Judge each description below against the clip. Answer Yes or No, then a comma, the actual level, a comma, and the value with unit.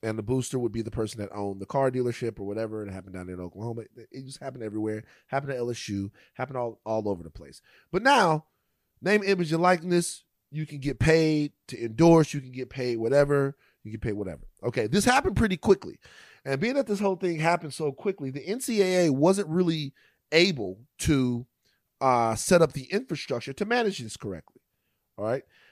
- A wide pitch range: Yes, wide, 6.8 semitones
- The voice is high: No, low, 135 Hz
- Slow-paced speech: No, average, 195 wpm